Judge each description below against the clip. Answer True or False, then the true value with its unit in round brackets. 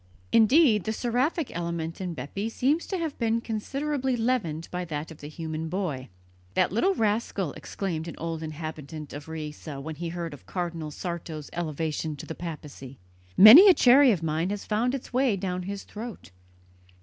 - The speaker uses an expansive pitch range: True (6.4 semitones)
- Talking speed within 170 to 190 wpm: True (175 wpm)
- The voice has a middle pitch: True (175 Hz)